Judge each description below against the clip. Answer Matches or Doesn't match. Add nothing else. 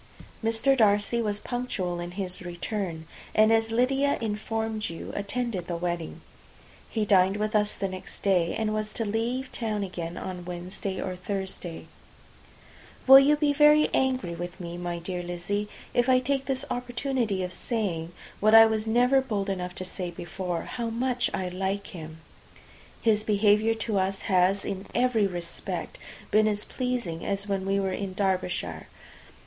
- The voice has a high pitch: Matches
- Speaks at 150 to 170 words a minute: Matches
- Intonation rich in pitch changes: Doesn't match